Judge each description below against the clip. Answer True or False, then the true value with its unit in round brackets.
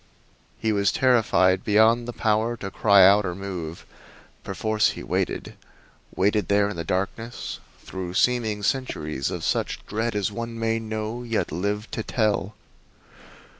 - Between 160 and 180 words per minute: False (145 wpm)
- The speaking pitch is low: True (105 Hz)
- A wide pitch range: False (2.7 semitones)